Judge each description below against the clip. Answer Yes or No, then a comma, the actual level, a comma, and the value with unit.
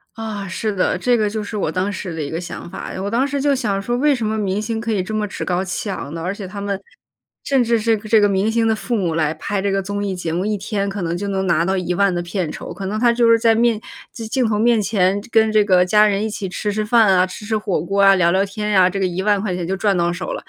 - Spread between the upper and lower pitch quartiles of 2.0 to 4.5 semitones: Yes, average, 2.7 semitones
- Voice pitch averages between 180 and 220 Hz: Yes, high, 200 Hz